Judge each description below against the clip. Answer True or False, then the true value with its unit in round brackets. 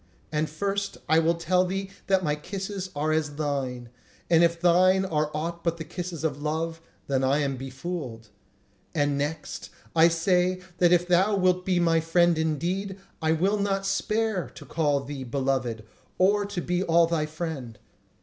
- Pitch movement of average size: True (3.5 semitones)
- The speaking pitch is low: False (165 Hz)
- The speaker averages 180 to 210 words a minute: False (170 wpm)